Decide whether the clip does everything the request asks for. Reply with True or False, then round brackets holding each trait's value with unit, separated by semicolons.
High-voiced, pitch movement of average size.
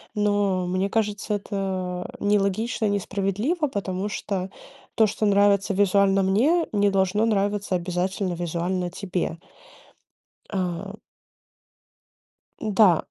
False (195 Hz; 1.9 semitones)